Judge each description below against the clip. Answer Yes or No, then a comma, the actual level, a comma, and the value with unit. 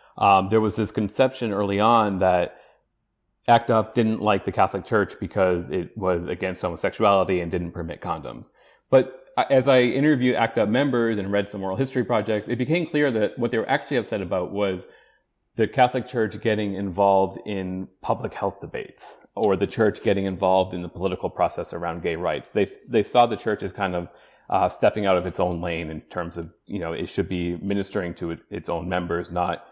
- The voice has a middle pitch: No, low, 100 Hz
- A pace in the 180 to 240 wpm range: Yes, average, 200 wpm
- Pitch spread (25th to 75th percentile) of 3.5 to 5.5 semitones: Yes, average, 4.2 semitones